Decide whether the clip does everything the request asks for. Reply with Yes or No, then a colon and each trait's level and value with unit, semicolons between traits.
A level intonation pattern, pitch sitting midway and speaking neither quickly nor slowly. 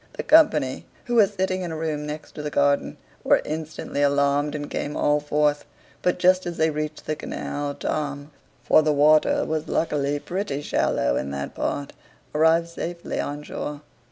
Yes: narrow, 2.0 semitones; medium, 150 Hz; average, 170 wpm